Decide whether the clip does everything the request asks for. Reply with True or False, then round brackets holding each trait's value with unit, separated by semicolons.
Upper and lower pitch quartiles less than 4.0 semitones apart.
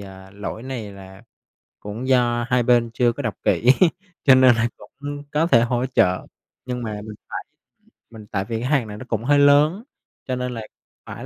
True (3.2 semitones)